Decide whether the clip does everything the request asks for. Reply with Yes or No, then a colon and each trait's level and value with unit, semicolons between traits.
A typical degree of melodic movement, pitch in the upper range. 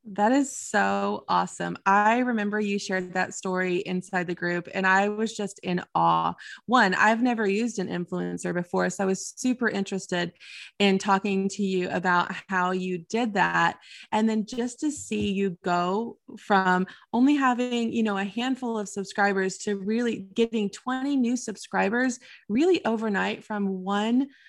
Yes: average, 3.8 semitones; high, 200 Hz